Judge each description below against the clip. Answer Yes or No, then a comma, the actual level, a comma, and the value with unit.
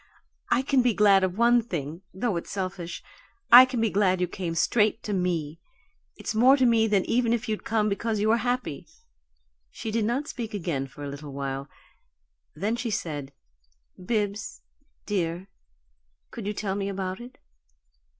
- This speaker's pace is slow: No, average, 170 wpm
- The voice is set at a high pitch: Yes, high, 205 Hz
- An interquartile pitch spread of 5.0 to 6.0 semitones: No, average, 4.6 semitones